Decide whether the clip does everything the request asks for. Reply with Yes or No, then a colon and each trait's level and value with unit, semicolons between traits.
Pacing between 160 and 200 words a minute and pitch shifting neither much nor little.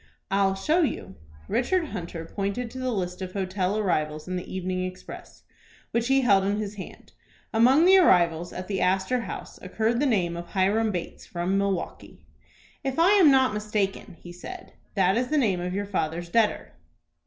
Yes: average, 180 wpm; average, 4.7 semitones